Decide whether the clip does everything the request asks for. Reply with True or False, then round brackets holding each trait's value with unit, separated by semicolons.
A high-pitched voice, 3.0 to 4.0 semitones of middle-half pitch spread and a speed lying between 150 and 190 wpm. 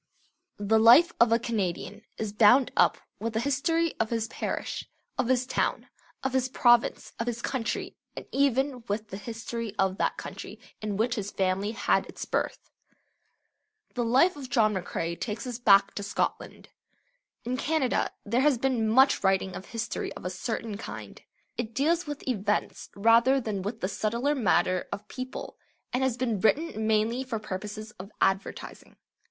True (230 Hz; 3.7 semitones; 170 wpm)